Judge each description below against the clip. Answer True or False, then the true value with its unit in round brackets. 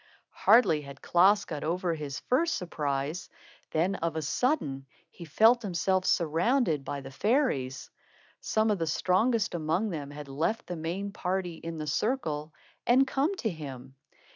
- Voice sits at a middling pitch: True (170 Hz)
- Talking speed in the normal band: True (155 wpm)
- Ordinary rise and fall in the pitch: False (6.3 semitones)